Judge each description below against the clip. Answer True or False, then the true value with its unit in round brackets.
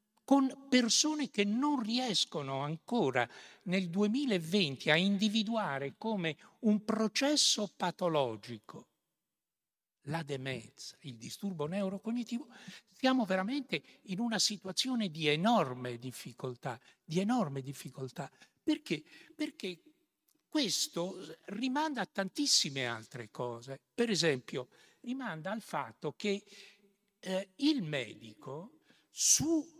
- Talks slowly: True (95 wpm)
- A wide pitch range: True (8.0 semitones)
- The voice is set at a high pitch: True (200 Hz)